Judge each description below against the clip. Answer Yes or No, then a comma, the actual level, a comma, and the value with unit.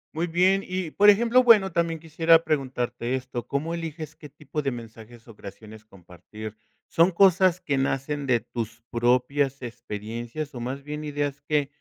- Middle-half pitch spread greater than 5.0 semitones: Yes, wide, 5.5 semitones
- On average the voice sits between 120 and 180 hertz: Yes, medium, 140 Hz